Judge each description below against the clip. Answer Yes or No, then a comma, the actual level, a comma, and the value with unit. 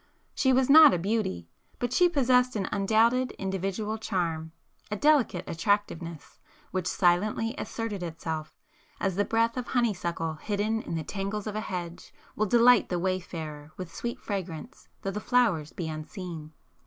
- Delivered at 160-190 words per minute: No, average, 150 wpm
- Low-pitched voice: No, high, 195 Hz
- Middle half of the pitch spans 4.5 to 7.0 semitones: Yes, average, 5.1 semitones